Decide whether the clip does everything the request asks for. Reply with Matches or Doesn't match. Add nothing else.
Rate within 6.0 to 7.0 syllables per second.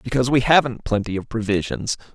Matches